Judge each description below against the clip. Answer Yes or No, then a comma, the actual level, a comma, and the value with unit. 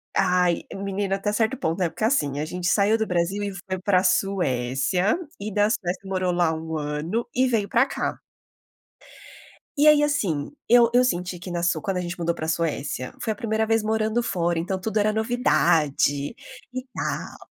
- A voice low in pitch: No, high, 190 Hz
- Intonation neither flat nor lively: Yes, average, 4.3 semitones